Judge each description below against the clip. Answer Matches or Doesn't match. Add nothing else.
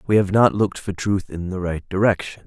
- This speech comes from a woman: Doesn't match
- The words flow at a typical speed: Doesn't match